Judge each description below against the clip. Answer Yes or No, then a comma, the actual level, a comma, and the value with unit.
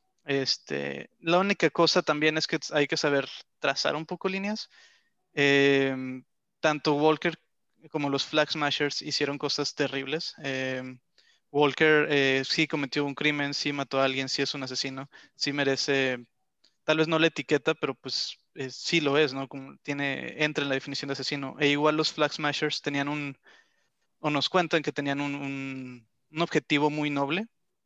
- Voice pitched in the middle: Yes, medium, 145 Hz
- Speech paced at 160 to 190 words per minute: Yes, average, 170 wpm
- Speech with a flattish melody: Yes, narrow, 2.3 semitones